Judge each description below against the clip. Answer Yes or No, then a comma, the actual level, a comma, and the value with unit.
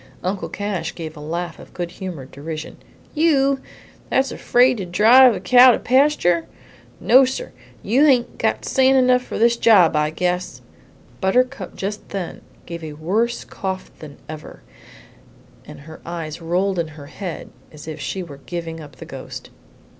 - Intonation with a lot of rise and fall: Yes, wide, 7.4 semitones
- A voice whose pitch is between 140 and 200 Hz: Yes, medium, 185 Hz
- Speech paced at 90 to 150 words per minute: No, average, 160 wpm